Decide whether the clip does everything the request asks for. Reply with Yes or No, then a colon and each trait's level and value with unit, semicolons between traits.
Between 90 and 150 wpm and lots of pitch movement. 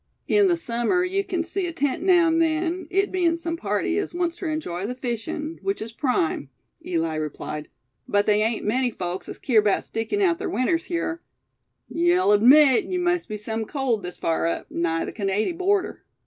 No: average, 195 wpm; wide, 8.8 semitones